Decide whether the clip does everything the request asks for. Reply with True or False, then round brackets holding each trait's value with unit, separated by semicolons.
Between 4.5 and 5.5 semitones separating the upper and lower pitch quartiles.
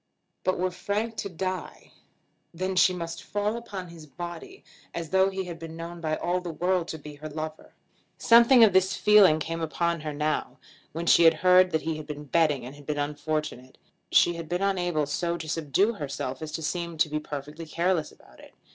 False (3.3 semitones)